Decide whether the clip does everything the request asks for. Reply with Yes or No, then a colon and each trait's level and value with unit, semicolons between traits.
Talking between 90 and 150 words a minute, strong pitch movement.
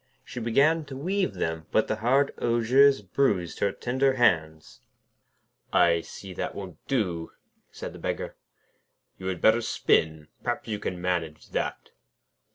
Yes: average, 145 wpm; wide, 7.2 semitones